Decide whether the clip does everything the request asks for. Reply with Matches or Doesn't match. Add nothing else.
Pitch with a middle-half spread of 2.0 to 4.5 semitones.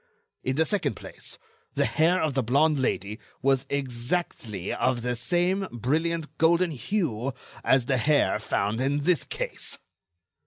Doesn't match